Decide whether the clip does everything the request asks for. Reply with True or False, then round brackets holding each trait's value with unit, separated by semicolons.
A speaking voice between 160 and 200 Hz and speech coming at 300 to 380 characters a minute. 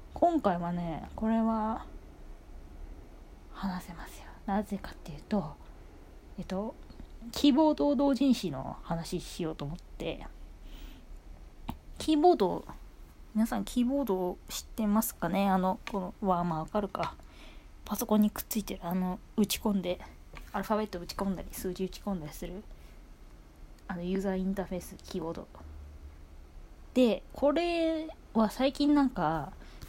False (190 Hz; 285 characters per minute)